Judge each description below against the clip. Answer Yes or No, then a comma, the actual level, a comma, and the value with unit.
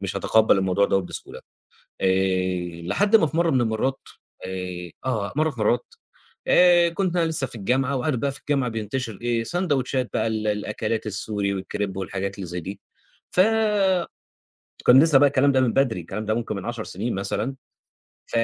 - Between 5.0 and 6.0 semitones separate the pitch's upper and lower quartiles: Yes, wide, 5.6 semitones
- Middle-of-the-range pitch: No, low, 115 Hz